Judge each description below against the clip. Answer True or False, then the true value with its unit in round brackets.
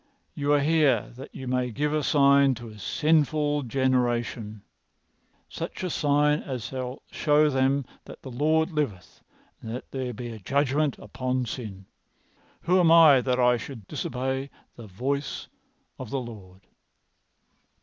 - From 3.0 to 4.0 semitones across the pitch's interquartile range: True (3.3 semitones)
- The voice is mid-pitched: False (130 Hz)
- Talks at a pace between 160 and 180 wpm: False (145 wpm)